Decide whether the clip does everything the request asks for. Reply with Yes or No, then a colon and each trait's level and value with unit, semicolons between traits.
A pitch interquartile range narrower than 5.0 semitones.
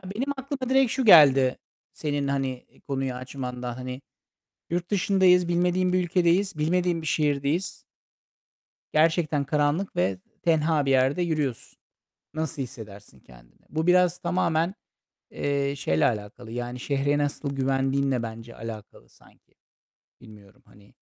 No: wide, 5.4 semitones